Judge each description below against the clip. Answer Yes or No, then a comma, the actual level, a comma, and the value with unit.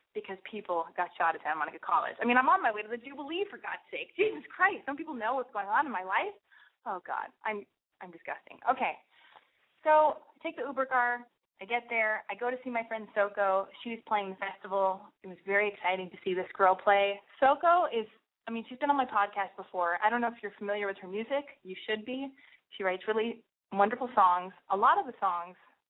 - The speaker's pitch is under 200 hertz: No, high, 215 Hz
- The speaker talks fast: Yes, fast, 225 wpm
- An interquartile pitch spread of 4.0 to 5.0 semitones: Yes, average, 4.6 semitones